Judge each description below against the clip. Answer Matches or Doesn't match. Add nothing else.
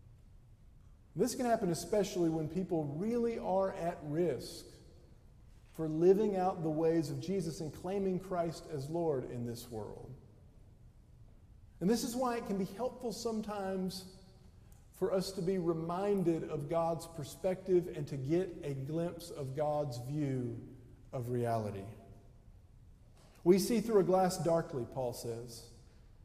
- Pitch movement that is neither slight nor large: Doesn't match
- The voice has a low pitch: Doesn't match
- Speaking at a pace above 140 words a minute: Doesn't match